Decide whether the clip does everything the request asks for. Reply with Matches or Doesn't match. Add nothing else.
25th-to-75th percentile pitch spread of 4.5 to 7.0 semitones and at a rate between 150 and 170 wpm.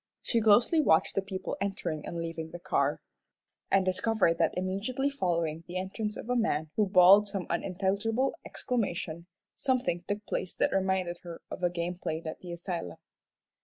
Doesn't match